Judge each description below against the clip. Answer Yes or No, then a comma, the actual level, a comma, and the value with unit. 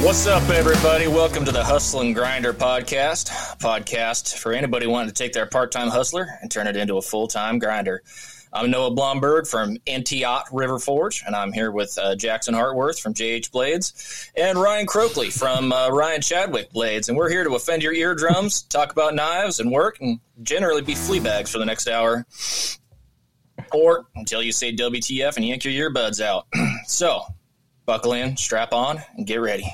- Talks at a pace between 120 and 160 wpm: No, average, 180 wpm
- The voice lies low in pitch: Yes, low, 125 Hz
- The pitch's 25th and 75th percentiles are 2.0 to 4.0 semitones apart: No, average, 4.5 semitones